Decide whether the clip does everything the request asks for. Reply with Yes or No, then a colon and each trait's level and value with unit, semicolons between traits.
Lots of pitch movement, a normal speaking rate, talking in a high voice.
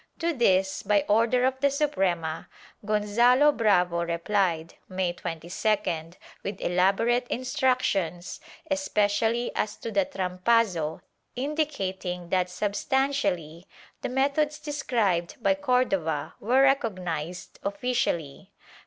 No: wide, 6.0 semitones; slow, 100 wpm; high, 205 Hz